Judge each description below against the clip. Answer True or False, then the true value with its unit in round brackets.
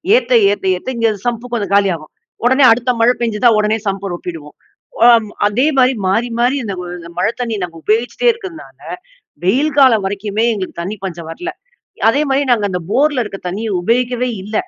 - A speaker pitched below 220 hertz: False (225 Hz)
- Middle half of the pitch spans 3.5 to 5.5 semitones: True (4.1 semitones)